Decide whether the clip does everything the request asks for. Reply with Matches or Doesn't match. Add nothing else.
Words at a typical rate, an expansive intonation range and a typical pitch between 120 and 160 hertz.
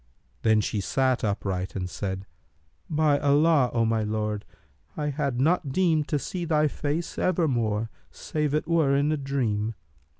Matches